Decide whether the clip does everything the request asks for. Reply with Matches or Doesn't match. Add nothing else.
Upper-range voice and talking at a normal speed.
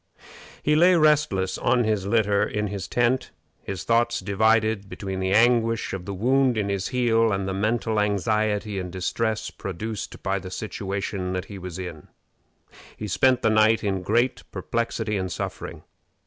Doesn't match